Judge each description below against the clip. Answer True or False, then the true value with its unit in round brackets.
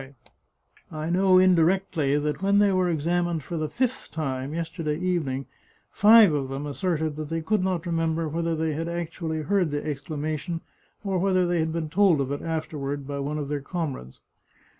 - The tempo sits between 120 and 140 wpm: False (180 wpm)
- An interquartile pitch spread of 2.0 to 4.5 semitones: True (3.2 semitones)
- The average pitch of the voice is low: False (160 Hz)